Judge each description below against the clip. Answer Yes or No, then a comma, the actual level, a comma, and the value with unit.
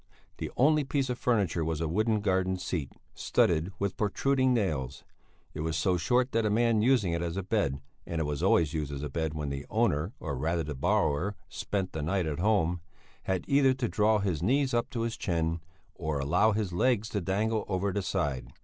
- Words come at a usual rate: No, fast, 210 wpm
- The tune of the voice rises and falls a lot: Yes, wide, 5.7 semitones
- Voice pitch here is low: Yes, very low, 95 Hz